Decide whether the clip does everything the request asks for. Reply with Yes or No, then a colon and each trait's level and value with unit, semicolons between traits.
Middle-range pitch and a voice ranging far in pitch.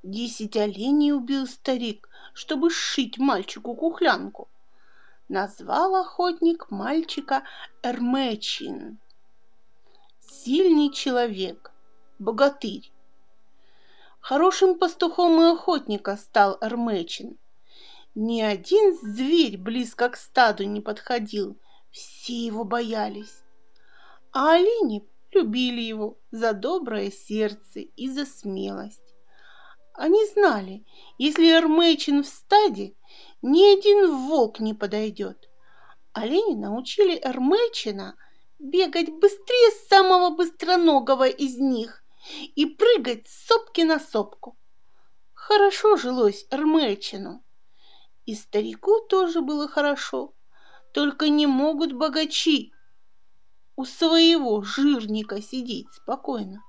No: very high, 270 Hz; wide, 7.7 semitones